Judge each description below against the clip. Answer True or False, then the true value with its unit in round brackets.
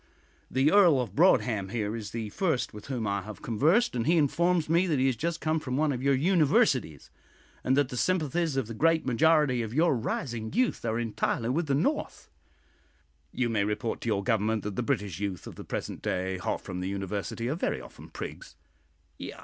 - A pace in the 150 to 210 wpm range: True (205 wpm)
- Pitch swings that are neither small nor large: False (6.5 semitones)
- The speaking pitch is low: True (125 Hz)